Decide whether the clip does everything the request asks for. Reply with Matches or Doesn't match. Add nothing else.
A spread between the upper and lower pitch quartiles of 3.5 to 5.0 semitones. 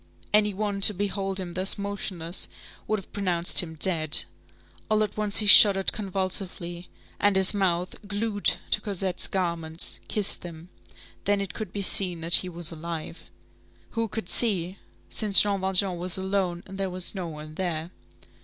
Doesn't match